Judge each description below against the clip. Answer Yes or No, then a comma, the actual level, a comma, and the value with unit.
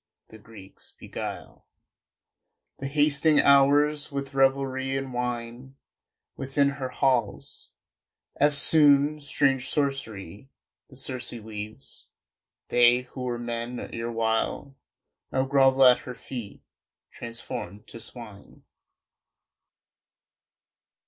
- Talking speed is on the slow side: Yes, slow, 90 wpm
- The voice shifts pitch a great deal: No, average, 2.9 semitones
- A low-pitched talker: Yes, low, 130 Hz